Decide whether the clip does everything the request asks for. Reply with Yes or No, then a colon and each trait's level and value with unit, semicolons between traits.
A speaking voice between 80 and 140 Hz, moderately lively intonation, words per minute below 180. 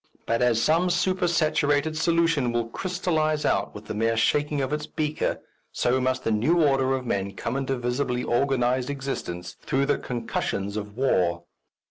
Yes: low, 135 Hz; average, 4.8 semitones; average, 160 wpm